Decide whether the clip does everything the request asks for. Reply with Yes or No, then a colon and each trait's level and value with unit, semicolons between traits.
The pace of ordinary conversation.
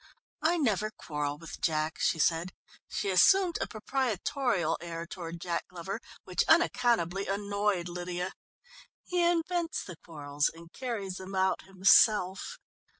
No: slow, 130 wpm